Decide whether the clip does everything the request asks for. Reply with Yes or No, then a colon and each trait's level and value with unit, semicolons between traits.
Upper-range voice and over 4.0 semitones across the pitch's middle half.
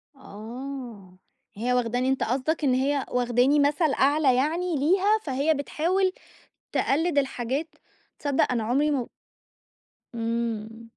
No: very high, 270 Hz; average, 3.7 semitones